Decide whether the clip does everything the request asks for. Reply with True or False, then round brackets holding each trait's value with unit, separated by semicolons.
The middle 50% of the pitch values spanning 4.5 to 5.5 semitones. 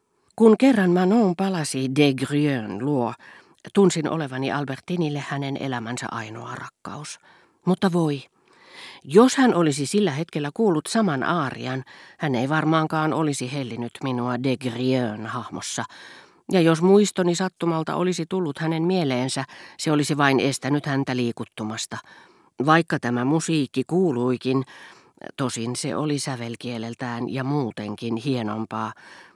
True (5.1 semitones)